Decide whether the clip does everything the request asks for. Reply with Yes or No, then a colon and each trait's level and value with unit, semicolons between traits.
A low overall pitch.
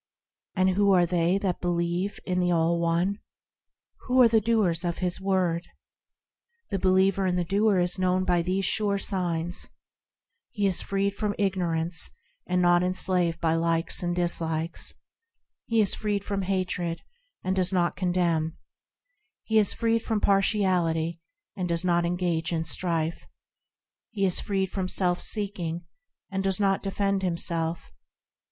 No: medium, 180 Hz